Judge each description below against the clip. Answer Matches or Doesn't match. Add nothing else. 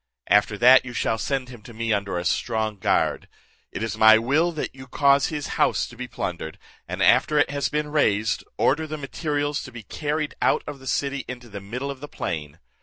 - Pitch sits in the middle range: Doesn't match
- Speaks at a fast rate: Matches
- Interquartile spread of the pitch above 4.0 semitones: Matches